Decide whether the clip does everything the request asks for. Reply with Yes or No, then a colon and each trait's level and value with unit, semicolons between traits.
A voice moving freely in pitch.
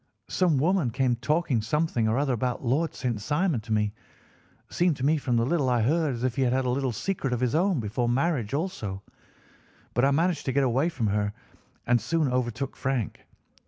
No: average, 4.4 semitones